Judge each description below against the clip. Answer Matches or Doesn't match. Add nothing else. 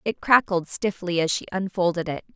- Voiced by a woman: Matches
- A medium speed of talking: Matches